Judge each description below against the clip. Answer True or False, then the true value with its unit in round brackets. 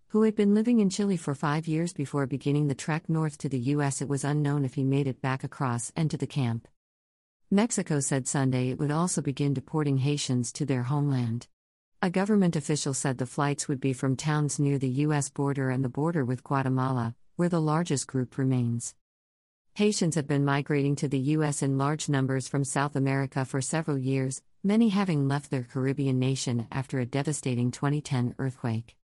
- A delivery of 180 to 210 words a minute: True (190 wpm)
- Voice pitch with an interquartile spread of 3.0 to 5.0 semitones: False (2.4 semitones)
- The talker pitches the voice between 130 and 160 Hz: True (140 Hz)